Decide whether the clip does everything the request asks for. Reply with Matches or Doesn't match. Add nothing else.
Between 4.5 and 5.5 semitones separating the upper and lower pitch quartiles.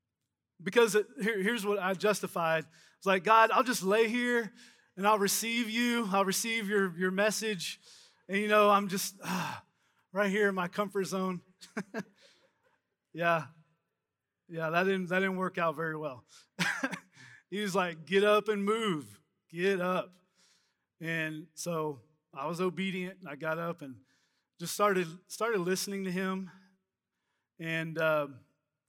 Doesn't match